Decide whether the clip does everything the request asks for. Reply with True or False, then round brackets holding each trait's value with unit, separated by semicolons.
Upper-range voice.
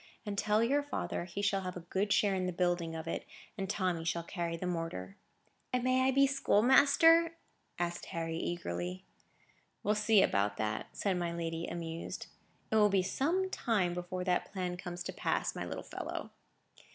False (180 Hz)